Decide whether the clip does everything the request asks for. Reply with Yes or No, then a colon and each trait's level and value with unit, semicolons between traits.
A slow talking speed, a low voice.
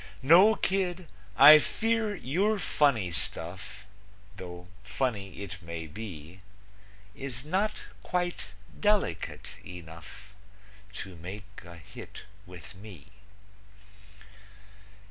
Yes: slow, 90 wpm; low, 105 Hz